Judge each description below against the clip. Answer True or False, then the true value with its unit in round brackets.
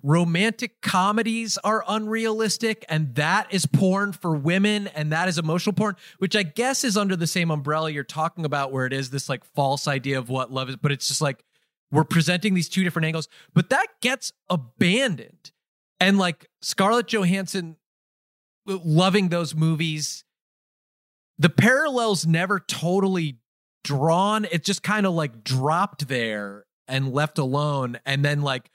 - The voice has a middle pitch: True (170 Hz)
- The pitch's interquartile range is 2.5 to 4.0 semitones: False (5.3 semitones)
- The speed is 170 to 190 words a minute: False (160 wpm)